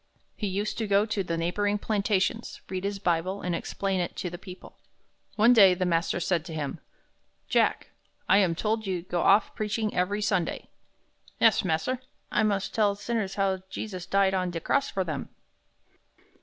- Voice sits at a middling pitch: No, high, 195 Hz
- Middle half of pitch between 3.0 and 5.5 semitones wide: No, narrow, 2.6 semitones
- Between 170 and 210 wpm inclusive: Yes, average, 180 wpm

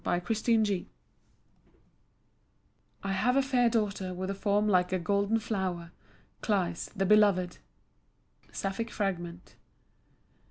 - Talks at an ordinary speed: No, slow, 110 wpm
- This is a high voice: Yes, high, 200 Hz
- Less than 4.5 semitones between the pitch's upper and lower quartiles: Yes, average, 2.8 semitones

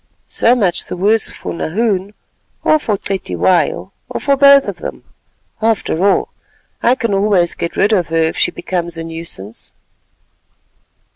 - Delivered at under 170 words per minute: Yes, average, 150 wpm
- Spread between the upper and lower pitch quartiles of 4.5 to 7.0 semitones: Yes, average, 4.8 semitones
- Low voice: No, high, 195 Hz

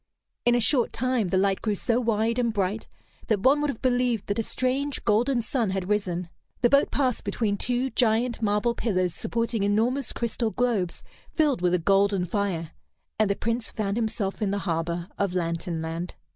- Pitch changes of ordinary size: Yes, average, 3.9 semitones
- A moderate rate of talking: Yes, average, 185 wpm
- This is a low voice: No, high, 215 Hz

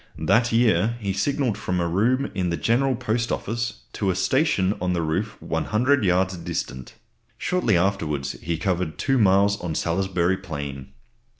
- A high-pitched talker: No, very low, 95 Hz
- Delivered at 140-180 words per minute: Yes, average, 160 wpm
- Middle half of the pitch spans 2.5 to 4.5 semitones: No, average, 5.2 semitones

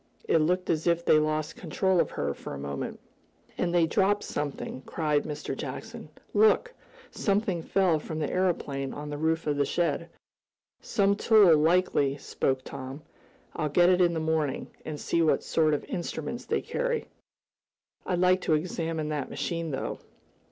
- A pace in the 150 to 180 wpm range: Yes, average, 165 wpm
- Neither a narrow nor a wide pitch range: Yes, average, 3.5 semitones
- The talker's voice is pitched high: No, medium, 160 Hz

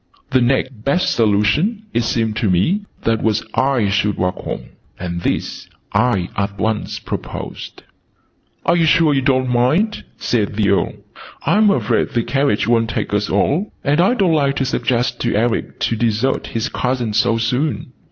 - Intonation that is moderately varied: Yes, average, 4.4 semitones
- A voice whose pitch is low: Yes, low, 120 Hz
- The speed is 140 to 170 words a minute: Yes, average, 165 wpm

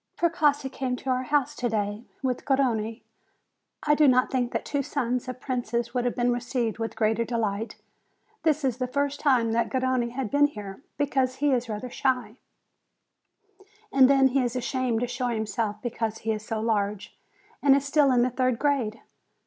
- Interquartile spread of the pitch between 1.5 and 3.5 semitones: Yes, average, 2.9 semitones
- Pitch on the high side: Yes, very high, 250 Hz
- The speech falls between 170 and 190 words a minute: Yes, average, 185 wpm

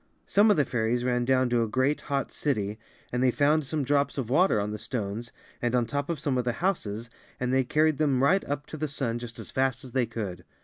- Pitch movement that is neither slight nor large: Yes, average, 3.6 semitones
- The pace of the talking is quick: Yes, fast, 250 wpm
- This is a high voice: No, low, 130 Hz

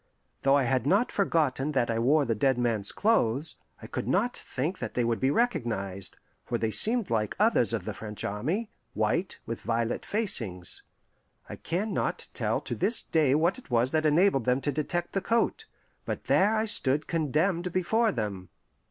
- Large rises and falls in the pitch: Yes, wide, 8.1 semitones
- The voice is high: No, medium, 140 Hz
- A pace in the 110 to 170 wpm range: No, average, 185 wpm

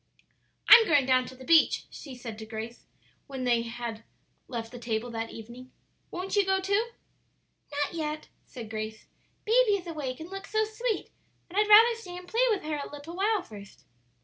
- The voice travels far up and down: Yes, wide, 8.8 semitones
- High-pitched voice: Yes, very high, 295 Hz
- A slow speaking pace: No, average, 190 wpm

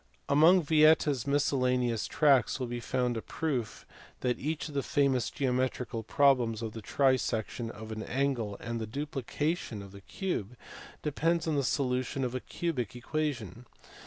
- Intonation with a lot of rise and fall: No, average, 3.8 semitones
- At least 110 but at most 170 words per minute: Yes, average, 160 wpm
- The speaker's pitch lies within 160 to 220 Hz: No, low, 130 Hz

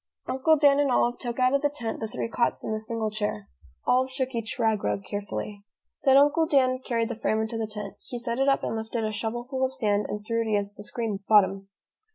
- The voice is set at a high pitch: Yes, high, 230 Hz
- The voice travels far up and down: No, average, 3.4 semitones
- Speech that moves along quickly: Yes, fast, 235 wpm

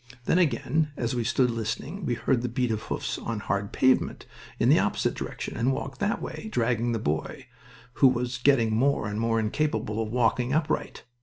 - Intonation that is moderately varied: Yes, average, 3.1 semitones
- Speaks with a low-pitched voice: Yes, low, 120 Hz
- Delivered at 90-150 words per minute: No, average, 190 wpm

